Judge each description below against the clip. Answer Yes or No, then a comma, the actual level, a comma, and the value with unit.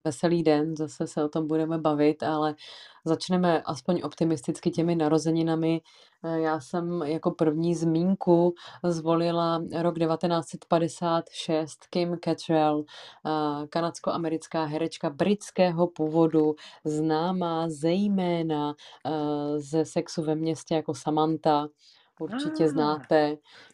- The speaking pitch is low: No, medium, 160 Hz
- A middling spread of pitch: No, narrow, 1.6 semitones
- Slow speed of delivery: Yes, slow, 95 wpm